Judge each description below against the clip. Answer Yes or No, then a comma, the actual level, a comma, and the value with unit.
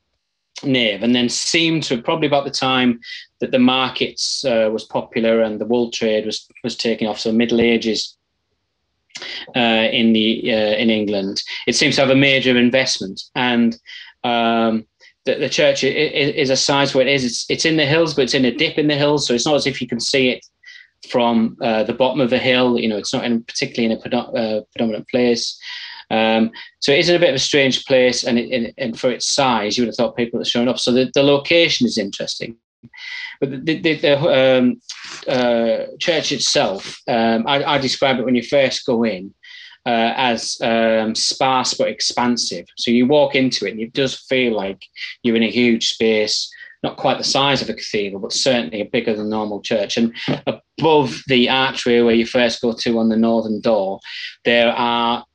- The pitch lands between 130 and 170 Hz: No, low, 120 Hz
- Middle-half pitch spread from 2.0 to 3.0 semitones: Yes, average, 2.7 semitones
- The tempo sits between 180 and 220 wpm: Yes, fast, 205 wpm